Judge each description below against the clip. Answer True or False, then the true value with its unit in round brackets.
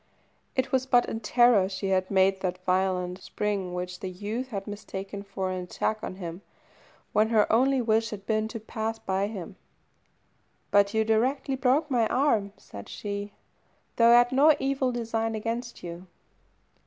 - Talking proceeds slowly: False (170 wpm)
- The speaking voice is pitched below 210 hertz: False (215 Hz)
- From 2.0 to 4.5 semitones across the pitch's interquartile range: True (3.9 semitones)